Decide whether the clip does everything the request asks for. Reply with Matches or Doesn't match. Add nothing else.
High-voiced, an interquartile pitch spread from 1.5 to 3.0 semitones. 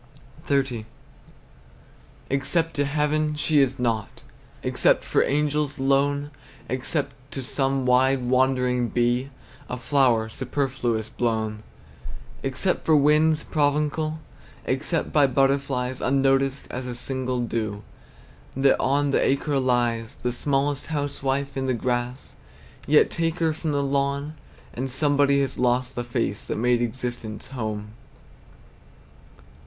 Doesn't match